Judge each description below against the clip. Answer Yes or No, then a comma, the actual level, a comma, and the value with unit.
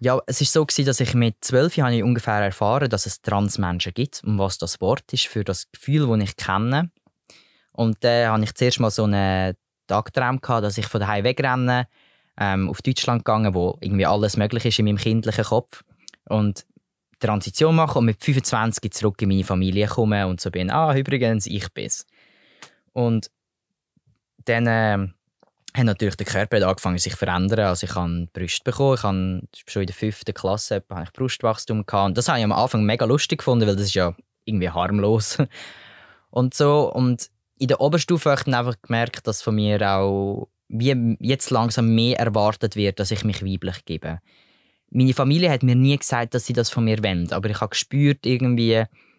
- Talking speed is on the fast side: Yes, fast, 195 wpm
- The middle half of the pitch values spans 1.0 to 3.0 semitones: No, average, 4.0 semitones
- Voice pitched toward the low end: Yes, low, 110 Hz